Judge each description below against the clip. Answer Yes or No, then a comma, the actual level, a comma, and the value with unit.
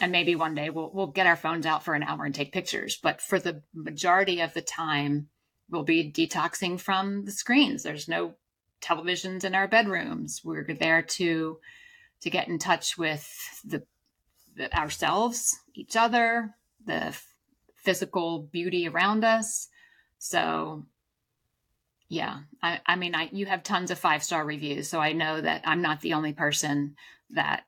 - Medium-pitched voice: Yes, medium, 170 Hz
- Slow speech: No, average, 165 wpm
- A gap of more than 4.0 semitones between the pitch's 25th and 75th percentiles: No, average, 3.7 semitones